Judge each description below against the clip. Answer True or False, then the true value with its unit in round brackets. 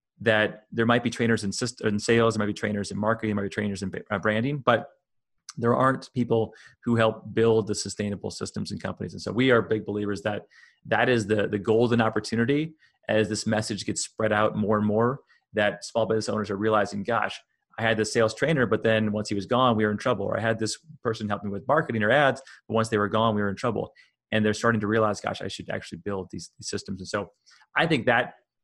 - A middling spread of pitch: False (1.7 semitones)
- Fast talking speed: True (235 wpm)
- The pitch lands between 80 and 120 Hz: True (110 Hz)